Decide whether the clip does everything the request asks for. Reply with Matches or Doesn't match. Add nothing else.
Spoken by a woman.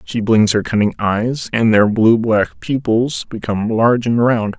Doesn't match